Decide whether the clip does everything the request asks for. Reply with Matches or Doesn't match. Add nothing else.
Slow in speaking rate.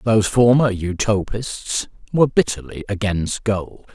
Matches